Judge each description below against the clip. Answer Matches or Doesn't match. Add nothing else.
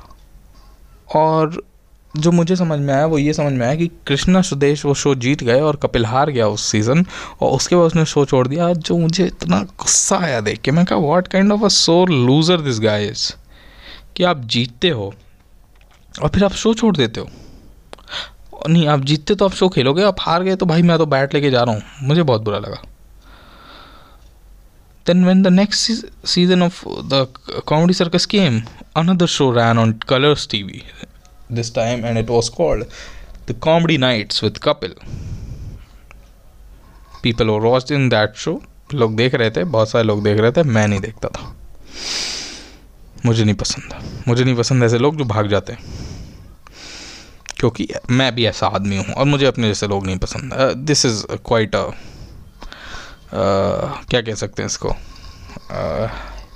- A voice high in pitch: Doesn't match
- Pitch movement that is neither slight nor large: Doesn't match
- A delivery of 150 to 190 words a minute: Matches